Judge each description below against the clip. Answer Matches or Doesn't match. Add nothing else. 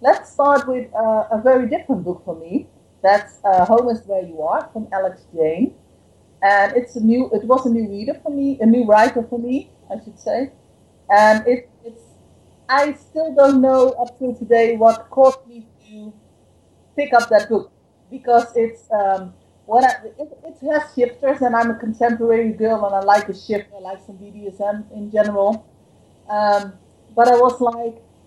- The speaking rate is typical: Matches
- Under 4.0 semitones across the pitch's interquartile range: Matches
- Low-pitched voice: Doesn't match